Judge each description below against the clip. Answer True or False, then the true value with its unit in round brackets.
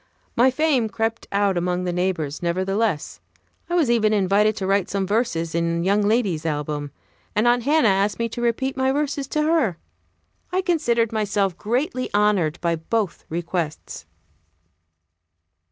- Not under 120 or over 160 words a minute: True (150 wpm)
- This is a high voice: True (210 Hz)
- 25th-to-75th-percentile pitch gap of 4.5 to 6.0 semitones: True (5.2 semitones)